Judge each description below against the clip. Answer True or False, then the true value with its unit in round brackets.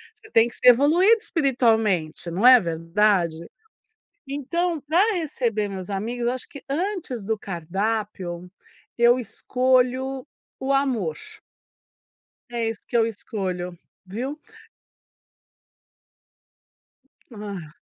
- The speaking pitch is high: True (230 Hz)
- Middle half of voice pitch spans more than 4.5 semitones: True (5.6 semitones)